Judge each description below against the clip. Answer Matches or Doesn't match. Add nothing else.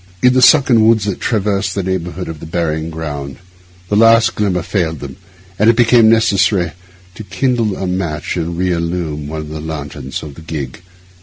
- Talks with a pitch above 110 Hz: Doesn't match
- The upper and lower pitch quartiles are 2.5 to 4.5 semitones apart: Doesn't match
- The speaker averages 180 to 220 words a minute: Matches